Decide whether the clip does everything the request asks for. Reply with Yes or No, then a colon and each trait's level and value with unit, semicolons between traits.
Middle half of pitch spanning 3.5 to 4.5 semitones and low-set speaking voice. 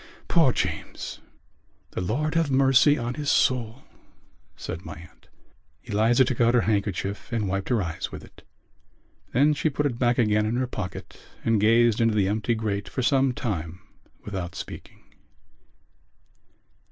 Yes: average, 4.1 semitones; low, 115 Hz